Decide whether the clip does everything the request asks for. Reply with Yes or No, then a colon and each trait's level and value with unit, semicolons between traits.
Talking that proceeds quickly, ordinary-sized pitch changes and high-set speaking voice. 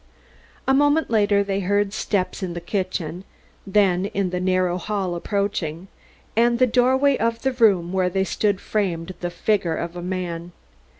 No: average, 165 wpm; average, 3.1 semitones; high, 195 Hz